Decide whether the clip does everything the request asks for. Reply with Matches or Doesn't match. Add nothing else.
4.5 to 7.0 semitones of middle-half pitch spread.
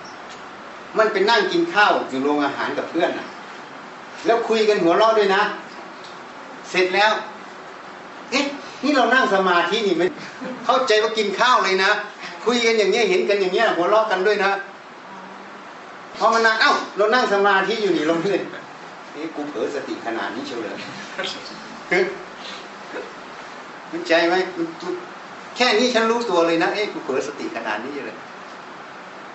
Doesn't match